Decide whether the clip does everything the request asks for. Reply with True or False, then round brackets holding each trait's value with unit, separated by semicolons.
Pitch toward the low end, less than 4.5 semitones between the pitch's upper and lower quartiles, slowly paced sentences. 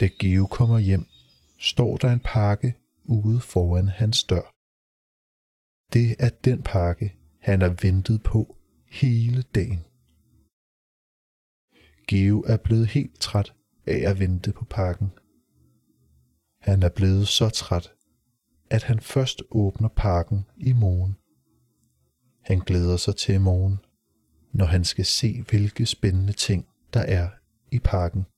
True (100 Hz; 3.9 semitones; 125 wpm)